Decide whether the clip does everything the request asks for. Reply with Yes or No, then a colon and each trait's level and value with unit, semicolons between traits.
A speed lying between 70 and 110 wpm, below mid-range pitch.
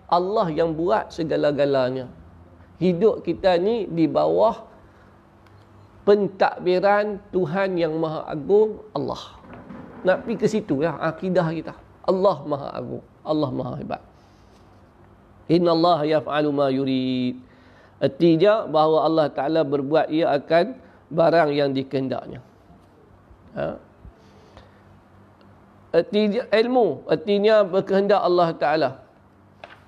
No: average, 100 wpm; medium, 160 Hz